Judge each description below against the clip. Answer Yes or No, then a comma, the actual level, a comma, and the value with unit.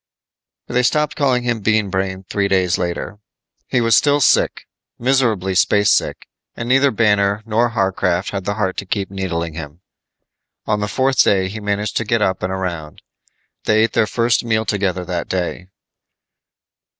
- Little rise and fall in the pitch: No, average, 3.5 semitones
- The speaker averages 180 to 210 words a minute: No, average, 160 wpm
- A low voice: Yes, low, 105 Hz